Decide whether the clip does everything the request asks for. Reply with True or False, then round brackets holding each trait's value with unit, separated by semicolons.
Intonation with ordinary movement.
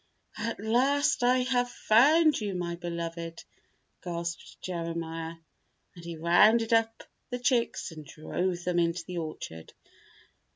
False (5.8 semitones)